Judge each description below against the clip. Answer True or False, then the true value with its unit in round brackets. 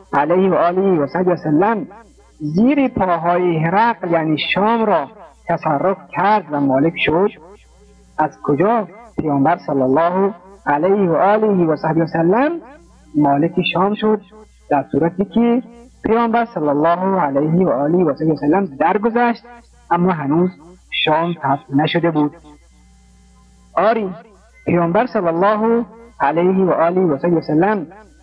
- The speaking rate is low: False (135 wpm)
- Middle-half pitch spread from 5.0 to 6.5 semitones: True (5.4 semitones)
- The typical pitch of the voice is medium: True (175 Hz)